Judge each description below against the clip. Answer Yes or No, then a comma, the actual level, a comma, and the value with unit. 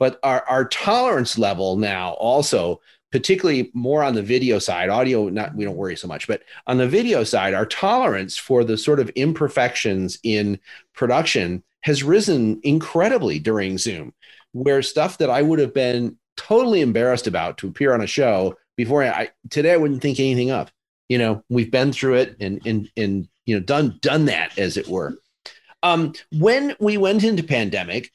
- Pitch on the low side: Yes, low, 130 Hz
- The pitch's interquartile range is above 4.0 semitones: Yes, average, 5.2 semitones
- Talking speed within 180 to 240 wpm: Yes, average, 185 wpm